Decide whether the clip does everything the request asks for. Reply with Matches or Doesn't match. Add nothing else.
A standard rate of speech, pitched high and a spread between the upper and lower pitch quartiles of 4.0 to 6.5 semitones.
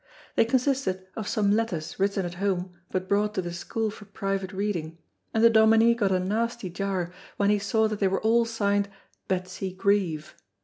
Doesn't match